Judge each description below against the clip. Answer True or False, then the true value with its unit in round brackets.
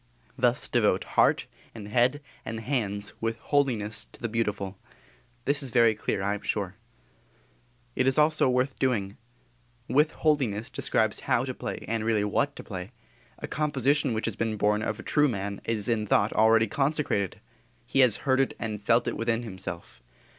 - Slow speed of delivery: False (175 wpm)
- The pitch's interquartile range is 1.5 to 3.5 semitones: False (4.1 semitones)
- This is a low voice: True (115 Hz)